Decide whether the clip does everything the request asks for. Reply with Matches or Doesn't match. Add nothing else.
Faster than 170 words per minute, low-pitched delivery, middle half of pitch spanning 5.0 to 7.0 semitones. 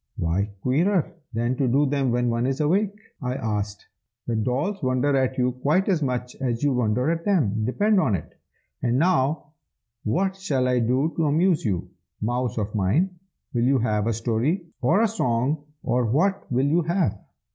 Matches